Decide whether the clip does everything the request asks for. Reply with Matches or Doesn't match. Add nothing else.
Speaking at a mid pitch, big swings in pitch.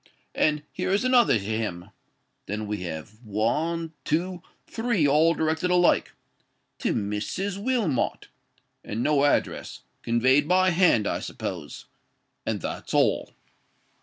Matches